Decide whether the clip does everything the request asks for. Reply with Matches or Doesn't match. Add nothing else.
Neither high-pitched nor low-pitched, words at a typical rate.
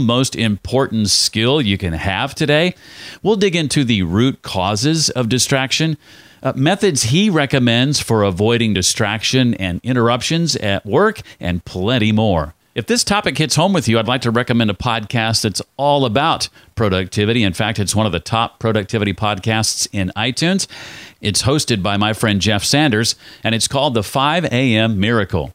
Doesn't match